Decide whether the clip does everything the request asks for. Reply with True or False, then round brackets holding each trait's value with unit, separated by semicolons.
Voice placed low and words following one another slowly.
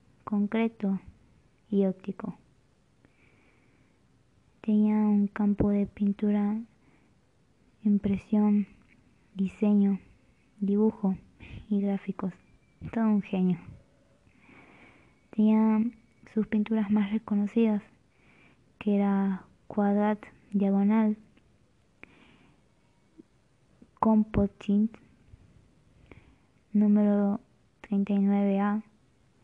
False (205 Hz; 55 wpm)